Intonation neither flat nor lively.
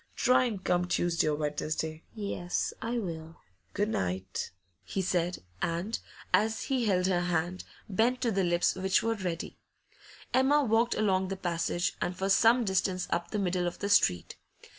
Yes: average, 3.8 semitones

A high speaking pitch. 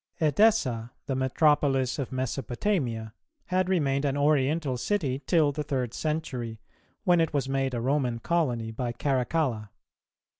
No: low, 135 Hz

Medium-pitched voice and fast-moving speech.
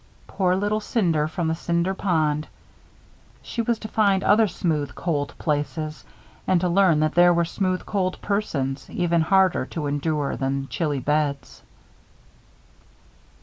No: medium, 170 Hz; average, 140 wpm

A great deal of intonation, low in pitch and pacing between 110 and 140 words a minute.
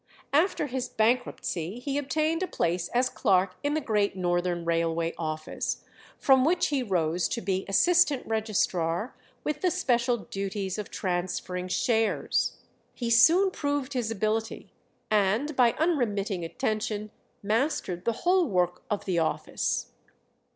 No: wide, 6.6 semitones; high, 220 Hz; slow, 135 wpm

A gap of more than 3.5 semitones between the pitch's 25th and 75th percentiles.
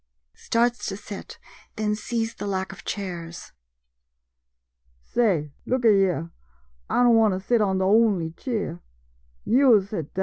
Yes: average, 4.0 semitones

